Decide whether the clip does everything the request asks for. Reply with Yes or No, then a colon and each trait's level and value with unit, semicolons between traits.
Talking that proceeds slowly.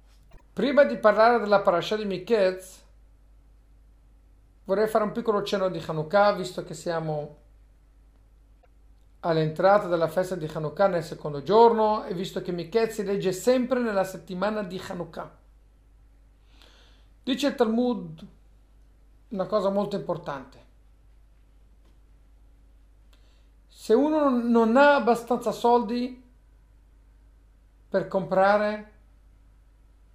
Yes: slow, 100 wpm